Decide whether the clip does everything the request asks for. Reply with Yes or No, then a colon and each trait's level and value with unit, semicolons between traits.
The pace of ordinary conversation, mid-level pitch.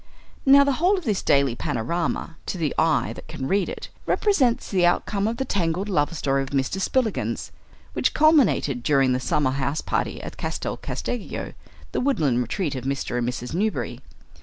Yes: average, 175 wpm; medium, 165 Hz